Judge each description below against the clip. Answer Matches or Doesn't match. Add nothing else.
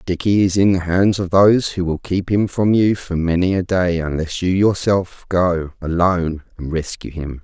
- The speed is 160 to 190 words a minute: Doesn't match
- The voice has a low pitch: Matches